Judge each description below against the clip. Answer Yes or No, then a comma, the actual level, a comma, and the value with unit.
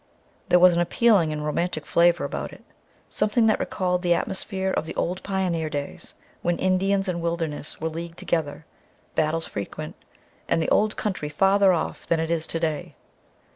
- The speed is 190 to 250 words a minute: No, average, 170 wpm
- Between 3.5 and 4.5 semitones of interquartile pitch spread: No, average, 2.9 semitones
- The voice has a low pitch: No, medium, 170 Hz